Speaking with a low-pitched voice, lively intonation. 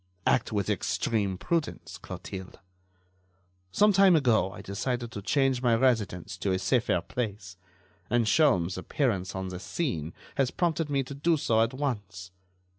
Yes: low, 115 Hz; wide, 6.4 semitones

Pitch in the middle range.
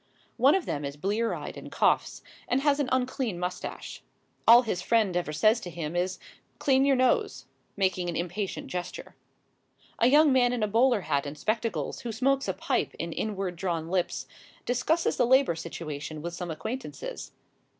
No: high, 215 Hz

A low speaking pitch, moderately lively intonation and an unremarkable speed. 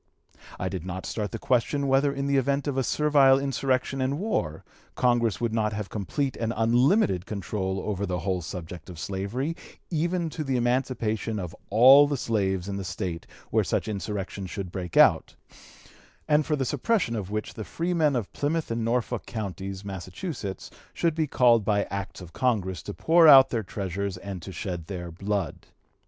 No: low, 110 Hz; wide, 6.1 semitones; average, 175 wpm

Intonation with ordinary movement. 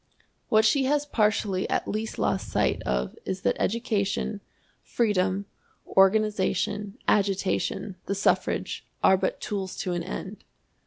No: narrow, 2.2 semitones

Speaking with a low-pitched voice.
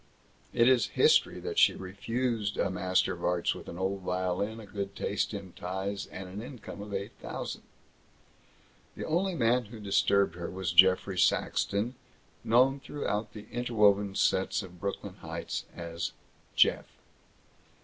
Yes: low, 100 Hz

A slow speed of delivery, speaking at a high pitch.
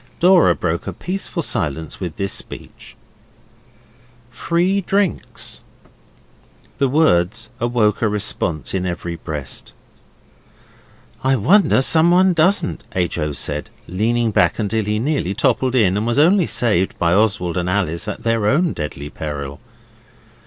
No: slow, 130 wpm; low, 110 Hz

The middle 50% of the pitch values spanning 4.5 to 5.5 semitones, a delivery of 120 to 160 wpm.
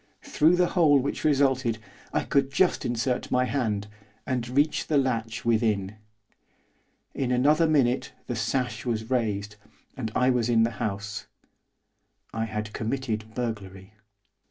No: average, 3.5 semitones; slow, 135 wpm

